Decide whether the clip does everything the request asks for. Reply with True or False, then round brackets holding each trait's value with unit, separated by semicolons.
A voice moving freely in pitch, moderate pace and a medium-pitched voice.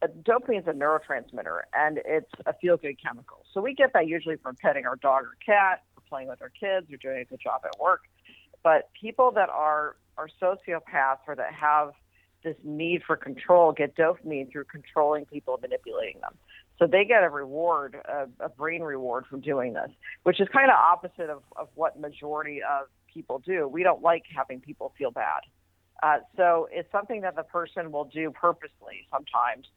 False (3.9 semitones; 190 wpm; 155 Hz)